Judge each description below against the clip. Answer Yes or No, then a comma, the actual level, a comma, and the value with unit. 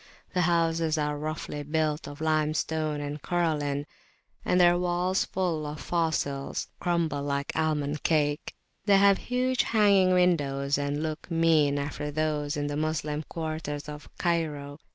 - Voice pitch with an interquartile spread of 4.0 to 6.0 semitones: No, narrow, 2.6 semitones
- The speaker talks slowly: No, average, 145 wpm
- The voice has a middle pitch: Yes, medium, 155 Hz